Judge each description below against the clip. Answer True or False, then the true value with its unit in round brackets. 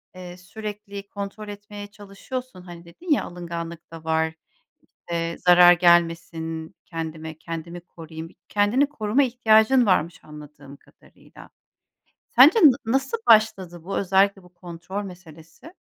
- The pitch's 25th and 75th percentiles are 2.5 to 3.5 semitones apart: False (4.0 semitones)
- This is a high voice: False (180 Hz)